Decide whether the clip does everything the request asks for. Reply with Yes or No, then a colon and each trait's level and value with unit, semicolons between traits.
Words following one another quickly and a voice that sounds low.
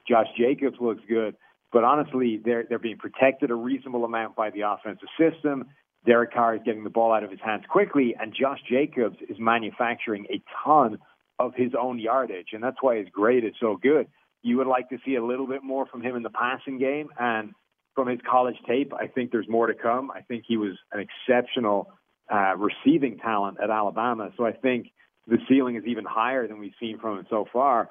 Yes: fast, 215 wpm; low, 120 Hz